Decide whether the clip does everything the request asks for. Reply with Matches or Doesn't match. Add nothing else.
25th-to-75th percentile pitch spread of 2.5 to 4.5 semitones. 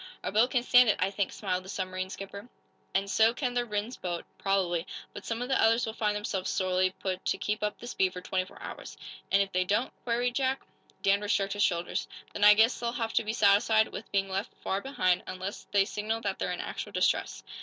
Matches